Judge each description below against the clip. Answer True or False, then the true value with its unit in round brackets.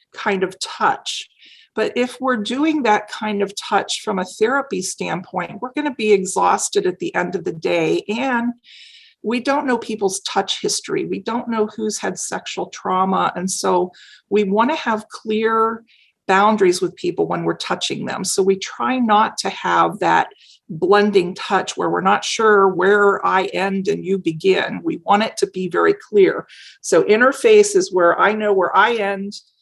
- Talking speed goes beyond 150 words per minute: True (180 wpm)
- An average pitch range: False (6.3 semitones)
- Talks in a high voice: True (215 Hz)